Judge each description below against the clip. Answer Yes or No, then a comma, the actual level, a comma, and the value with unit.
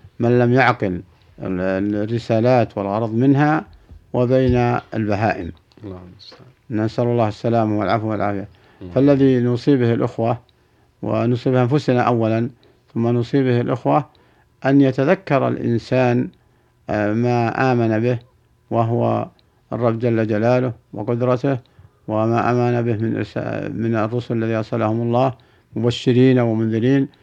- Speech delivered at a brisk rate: No, average, 95 wpm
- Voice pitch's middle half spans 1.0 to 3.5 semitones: Yes, narrow, 2.4 semitones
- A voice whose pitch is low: Yes, low, 120 Hz